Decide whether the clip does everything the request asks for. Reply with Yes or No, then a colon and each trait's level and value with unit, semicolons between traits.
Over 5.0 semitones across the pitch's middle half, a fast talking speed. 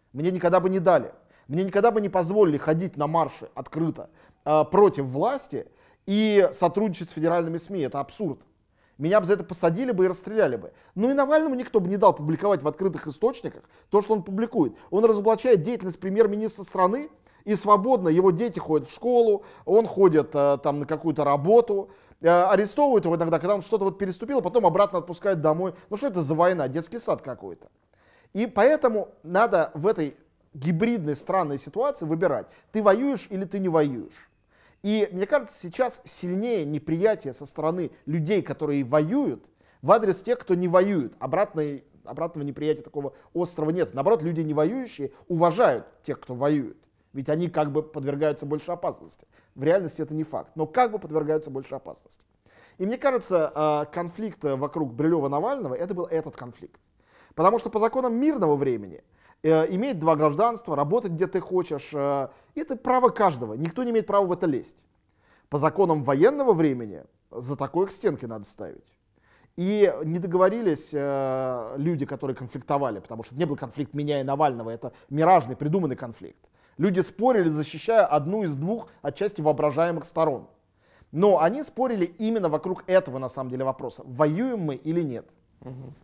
Yes: wide, 5.6 semitones; fast, 165 wpm